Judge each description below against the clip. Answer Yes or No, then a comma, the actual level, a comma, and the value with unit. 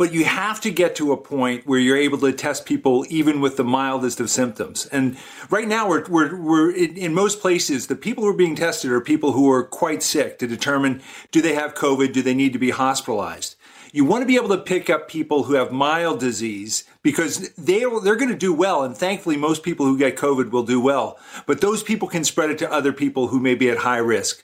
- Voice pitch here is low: No, medium, 145 Hz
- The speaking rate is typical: No, fast, 245 wpm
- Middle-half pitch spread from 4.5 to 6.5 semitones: Yes, average, 4.8 semitones